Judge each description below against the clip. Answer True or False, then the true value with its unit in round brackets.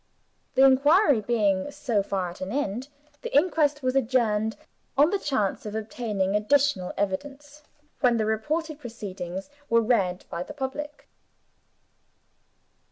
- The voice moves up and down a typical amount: False (5.9 semitones)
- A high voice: True (235 Hz)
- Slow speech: True (130 wpm)